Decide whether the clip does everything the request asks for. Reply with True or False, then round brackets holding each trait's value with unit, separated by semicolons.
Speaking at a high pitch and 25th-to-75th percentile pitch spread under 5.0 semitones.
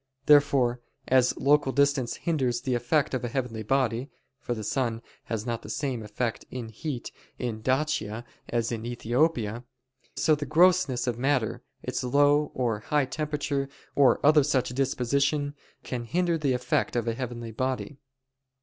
False (130 Hz; 3.3 semitones)